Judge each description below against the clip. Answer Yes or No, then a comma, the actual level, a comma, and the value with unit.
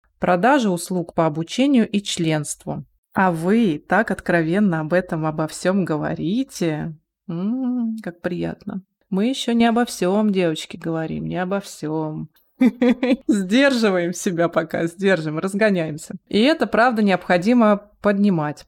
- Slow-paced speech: No, average, 120 wpm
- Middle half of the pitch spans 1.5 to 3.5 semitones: No, average, 4.9 semitones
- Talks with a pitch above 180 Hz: Yes, high, 190 Hz